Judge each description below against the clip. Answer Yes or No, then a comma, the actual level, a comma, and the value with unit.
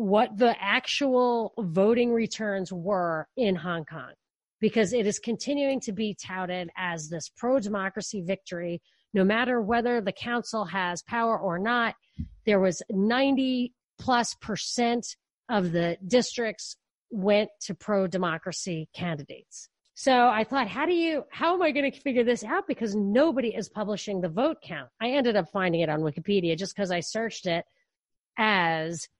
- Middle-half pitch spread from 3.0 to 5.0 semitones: Yes, average, 4.7 semitones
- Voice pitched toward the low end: No, high, 215 Hz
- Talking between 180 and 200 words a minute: No, average, 160 wpm